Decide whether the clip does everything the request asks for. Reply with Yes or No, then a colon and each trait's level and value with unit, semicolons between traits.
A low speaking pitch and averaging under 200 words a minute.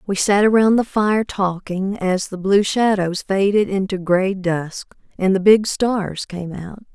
No: high, 195 Hz; average, 175 wpm